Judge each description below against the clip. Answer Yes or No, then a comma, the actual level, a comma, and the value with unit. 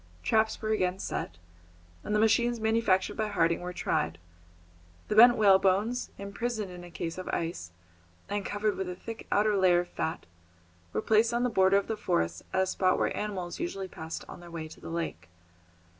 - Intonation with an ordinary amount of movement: Yes, average, 3.7 semitones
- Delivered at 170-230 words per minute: Yes, average, 190 wpm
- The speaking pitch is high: Yes, high, 195 Hz